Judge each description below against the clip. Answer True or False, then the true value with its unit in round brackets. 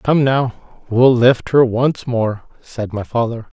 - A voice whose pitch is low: True (120 Hz)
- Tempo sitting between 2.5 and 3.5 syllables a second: True (3.4 syllables/s)